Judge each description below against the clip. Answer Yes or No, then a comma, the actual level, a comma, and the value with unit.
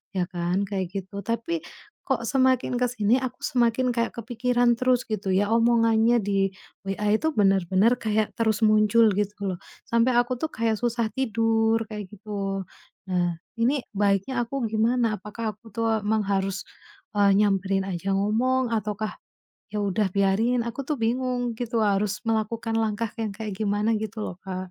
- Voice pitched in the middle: No, high, 220 Hz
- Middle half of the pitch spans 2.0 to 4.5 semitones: Yes, average, 2.8 semitones